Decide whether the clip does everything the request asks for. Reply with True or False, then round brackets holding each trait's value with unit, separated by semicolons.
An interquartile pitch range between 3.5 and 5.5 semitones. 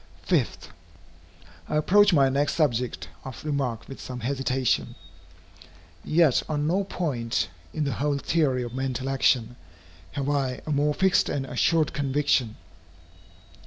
False (2.9 semitones)